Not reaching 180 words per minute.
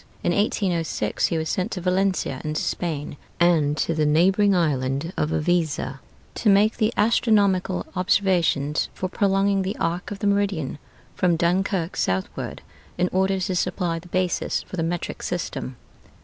Yes: average, 150 wpm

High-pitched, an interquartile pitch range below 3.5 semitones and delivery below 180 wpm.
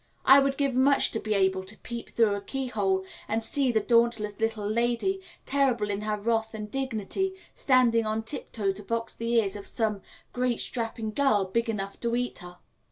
No: high, 225 Hz; average, 2.9 semitones; average, 190 wpm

